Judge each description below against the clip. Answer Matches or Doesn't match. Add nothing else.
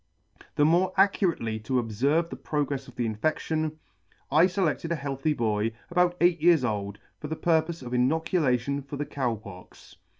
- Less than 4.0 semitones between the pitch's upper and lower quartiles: Doesn't match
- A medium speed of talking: Matches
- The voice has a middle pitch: Matches